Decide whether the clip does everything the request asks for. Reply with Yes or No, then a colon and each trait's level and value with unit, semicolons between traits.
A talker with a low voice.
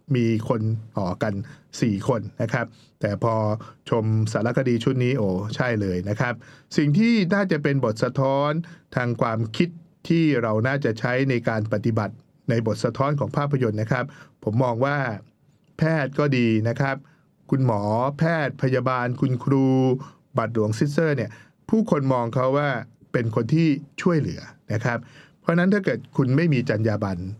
Yes: low, 130 Hz